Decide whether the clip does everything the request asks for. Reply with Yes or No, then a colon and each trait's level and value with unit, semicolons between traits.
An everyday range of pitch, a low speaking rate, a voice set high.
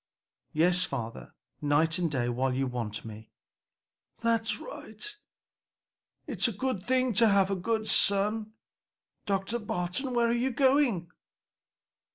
No: wide, 7.6 semitones; slow, 130 wpm; high, 195 Hz